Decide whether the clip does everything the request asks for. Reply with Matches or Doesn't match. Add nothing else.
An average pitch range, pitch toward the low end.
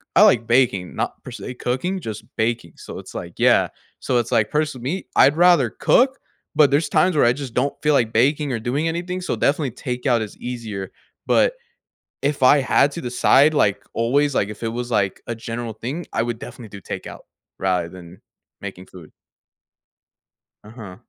Matches